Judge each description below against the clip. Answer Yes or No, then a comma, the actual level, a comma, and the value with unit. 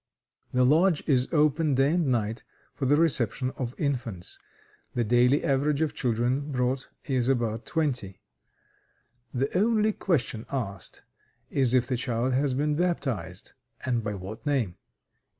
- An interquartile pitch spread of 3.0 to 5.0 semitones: Yes, average, 3.6 semitones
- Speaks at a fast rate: No, average, 140 wpm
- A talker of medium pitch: No, low, 130 Hz